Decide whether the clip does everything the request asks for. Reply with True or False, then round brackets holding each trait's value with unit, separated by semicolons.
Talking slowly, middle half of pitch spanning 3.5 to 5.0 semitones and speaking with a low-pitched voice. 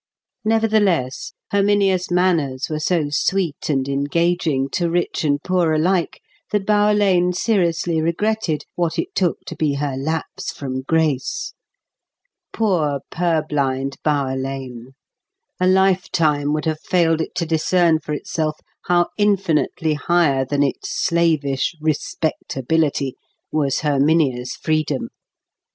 False (120 wpm; 3.9 semitones; 160 Hz)